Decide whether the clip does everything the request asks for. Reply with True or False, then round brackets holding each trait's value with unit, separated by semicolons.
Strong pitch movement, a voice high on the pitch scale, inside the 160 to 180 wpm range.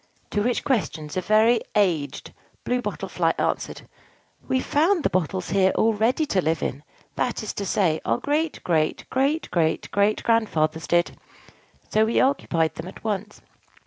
True (6.1 semitones; 205 Hz; 165 wpm)